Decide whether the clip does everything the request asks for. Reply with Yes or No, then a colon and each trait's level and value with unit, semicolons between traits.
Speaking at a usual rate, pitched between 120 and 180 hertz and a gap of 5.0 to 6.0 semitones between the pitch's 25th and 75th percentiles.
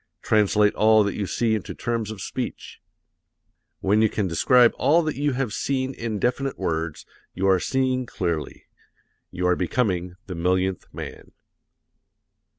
No: average, 150 wpm; low, 105 Hz; wide, 5.4 semitones